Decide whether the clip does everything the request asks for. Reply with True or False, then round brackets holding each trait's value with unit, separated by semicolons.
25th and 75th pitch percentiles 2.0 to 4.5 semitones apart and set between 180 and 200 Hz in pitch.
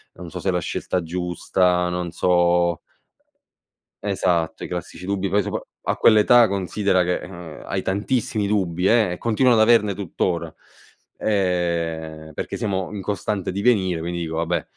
False (2.7 semitones; 90 Hz)